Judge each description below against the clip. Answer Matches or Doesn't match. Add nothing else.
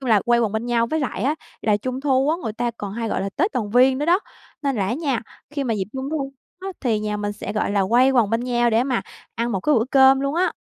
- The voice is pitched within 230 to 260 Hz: Matches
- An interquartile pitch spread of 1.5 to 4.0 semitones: Matches